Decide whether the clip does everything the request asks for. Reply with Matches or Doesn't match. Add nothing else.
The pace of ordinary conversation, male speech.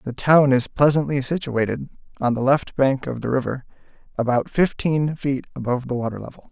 Matches